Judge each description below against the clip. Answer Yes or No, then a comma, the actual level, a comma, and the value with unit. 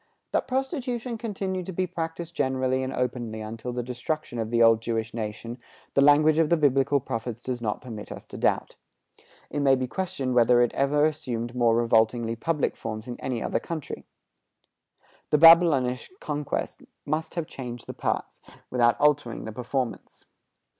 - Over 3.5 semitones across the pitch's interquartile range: Yes, average, 4.8 semitones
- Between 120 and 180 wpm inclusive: Yes, average, 165 wpm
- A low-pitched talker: Yes, low, 130 Hz